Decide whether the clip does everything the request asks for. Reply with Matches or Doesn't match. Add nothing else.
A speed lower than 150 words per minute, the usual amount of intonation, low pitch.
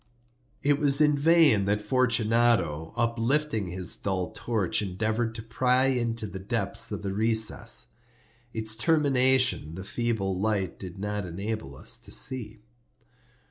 Matches